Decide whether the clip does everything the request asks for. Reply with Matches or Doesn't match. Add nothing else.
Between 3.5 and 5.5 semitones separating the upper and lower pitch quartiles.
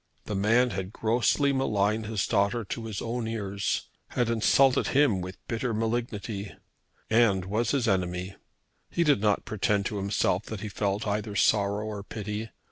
Doesn't match